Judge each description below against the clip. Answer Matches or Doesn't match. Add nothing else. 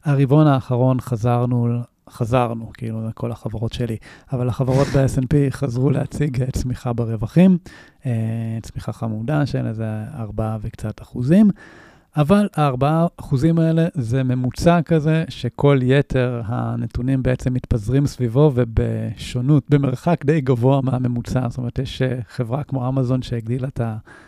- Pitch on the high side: Doesn't match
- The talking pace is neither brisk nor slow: Matches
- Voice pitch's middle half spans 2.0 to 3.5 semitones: Matches